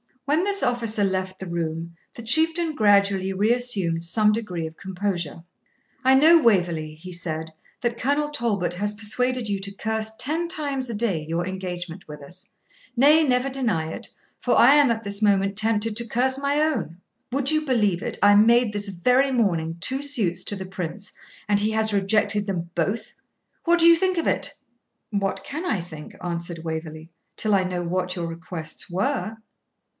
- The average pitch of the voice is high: Yes, high, 205 Hz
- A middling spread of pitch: No, wide, 6.0 semitones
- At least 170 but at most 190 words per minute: Yes, average, 180 wpm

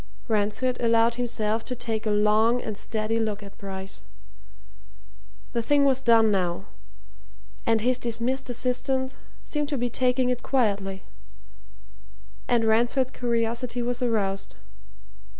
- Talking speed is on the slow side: Yes, slow, 125 wpm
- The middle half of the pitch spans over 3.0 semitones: No, average, 2.7 semitones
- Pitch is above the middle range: Yes, high, 230 Hz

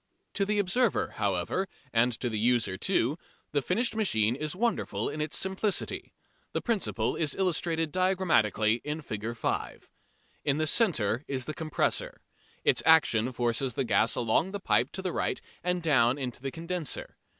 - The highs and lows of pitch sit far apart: Yes, wide, 7.6 semitones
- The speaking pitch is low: No, medium, 150 Hz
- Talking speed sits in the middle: Yes, average, 160 wpm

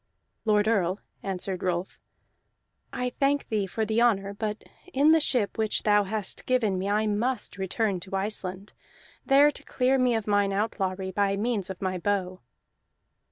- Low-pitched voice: No, high, 205 Hz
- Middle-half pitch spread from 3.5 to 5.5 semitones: No, average, 3.0 semitones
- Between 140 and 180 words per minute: Yes, average, 160 wpm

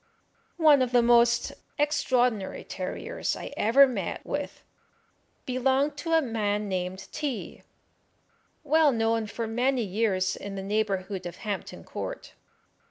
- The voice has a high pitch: Yes, high, 235 Hz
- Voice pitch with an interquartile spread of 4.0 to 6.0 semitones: Yes, average, 4.8 semitones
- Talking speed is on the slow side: Yes, slow, 130 wpm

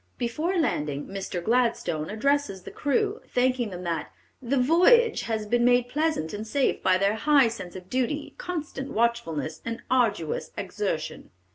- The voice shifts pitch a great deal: Yes, wide, 6.6 semitones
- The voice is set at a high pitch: Yes, high, 235 Hz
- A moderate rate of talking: Yes, average, 150 wpm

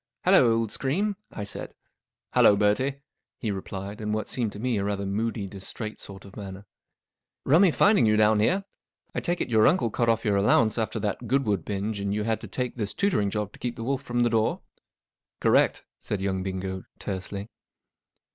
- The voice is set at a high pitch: No, low, 110 Hz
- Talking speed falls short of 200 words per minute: No, fast, 205 wpm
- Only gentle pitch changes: No, average, 3.1 semitones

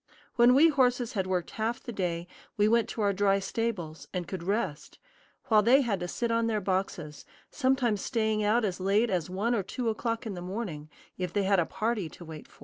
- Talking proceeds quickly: Yes, fast, 220 wpm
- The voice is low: No, high, 205 Hz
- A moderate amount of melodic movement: Yes, average, 4.0 semitones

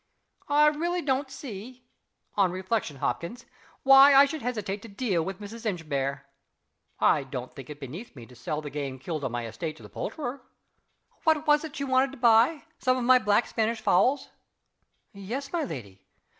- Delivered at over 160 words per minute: Yes, average, 180 wpm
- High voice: Yes, high, 225 Hz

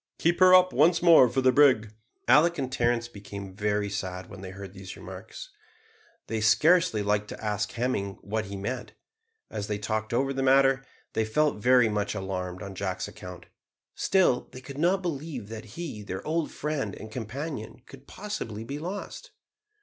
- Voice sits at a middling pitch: No, low, 115 Hz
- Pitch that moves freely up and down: Yes, wide, 6.2 semitones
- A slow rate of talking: No, average, 175 wpm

